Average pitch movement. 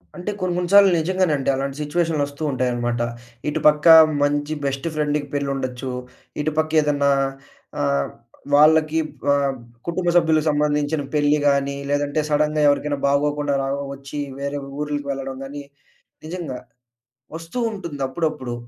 No: narrow, 2.0 semitones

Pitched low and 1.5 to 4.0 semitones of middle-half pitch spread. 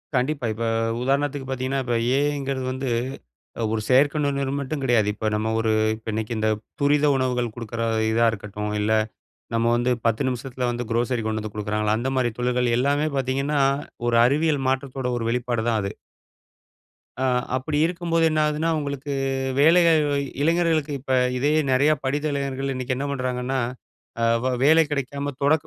Yes: low, 130 Hz; average, 3.1 semitones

